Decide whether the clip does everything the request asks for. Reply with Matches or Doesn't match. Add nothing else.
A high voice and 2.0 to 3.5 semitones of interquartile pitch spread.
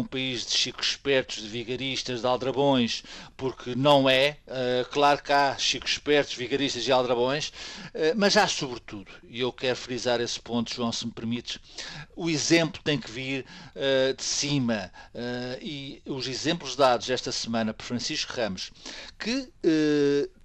Doesn't match